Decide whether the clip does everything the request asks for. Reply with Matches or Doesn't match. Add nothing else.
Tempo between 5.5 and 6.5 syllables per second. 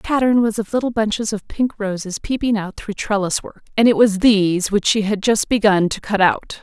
Doesn't match